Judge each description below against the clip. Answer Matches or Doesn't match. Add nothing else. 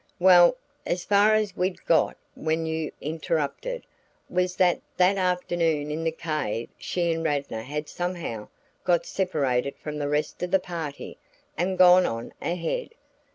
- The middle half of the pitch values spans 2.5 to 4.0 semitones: Matches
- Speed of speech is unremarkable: Matches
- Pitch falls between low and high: Matches